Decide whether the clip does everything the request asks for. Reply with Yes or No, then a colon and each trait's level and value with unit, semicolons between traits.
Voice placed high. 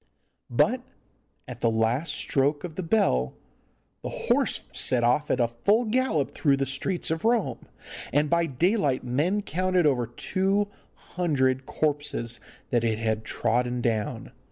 No: medium, 145 Hz